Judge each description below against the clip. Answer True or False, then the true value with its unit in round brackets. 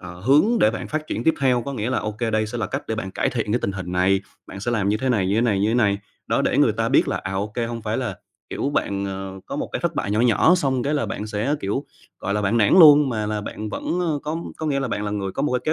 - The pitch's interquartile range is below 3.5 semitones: False (4.6 semitones)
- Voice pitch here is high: False (110 Hz)